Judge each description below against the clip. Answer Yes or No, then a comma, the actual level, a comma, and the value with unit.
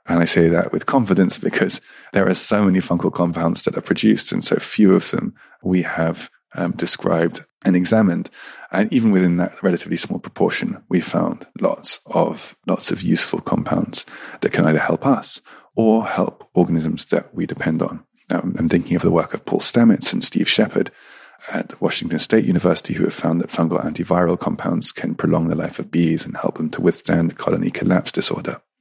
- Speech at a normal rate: Yes, average, 190 wpm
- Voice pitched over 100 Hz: No, very low, 85 Hz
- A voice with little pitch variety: Yes, narrow, 1.6 semitones